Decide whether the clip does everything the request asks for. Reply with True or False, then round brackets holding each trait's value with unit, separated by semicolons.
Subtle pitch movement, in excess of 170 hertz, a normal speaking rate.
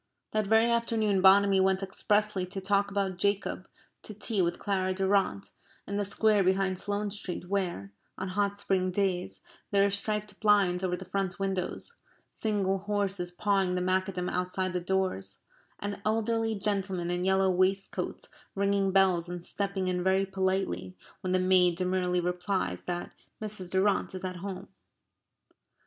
True (1.8 semitones; 190 Hz; 155 wpm)